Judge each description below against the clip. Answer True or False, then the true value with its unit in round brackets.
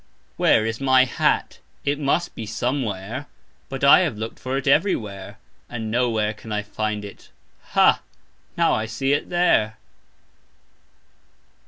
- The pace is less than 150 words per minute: True (140 wpm)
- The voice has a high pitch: False (115 Hz)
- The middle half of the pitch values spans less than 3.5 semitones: False (4.1 semitones)